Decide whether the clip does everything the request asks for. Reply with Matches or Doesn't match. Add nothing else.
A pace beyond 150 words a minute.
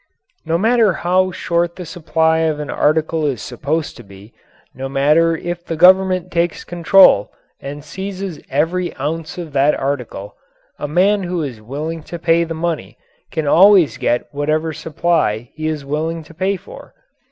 Matches